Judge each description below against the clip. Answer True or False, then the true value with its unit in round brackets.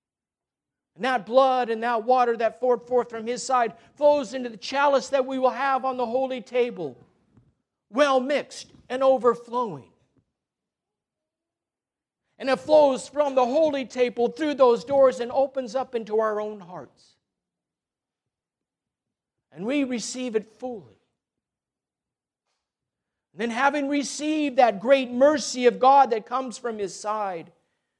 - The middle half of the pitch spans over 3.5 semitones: False (2.8 semitones)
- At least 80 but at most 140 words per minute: True (135 wpm)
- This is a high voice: True (250 Hz)